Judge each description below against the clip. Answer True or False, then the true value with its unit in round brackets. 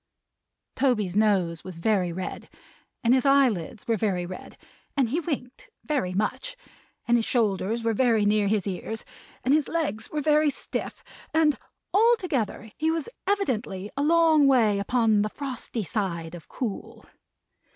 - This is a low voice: False (230 Hz)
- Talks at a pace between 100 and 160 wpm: True (150 wpm)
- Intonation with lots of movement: True (5.9 semitones)